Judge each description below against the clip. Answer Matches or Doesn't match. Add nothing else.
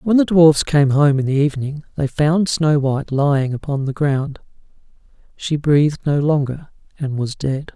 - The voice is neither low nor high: Matches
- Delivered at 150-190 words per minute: Matches